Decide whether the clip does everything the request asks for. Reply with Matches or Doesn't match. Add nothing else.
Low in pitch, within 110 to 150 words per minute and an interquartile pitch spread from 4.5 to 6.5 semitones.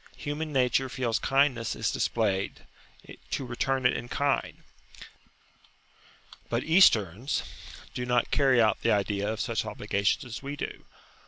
Doesn't match